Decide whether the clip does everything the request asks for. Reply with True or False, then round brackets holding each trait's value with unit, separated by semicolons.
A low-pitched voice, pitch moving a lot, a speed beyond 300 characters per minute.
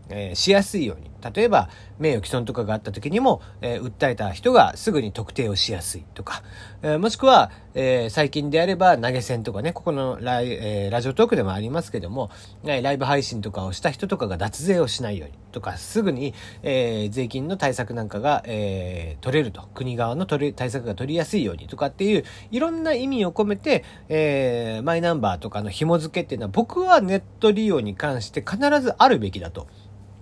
True (125 Hz; 8.7 semitones; 395 characters per minute)